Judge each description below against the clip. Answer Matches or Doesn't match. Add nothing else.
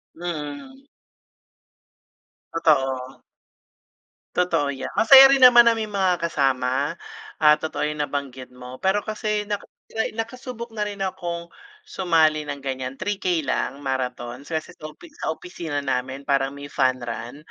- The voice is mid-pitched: Matches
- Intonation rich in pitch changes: Matches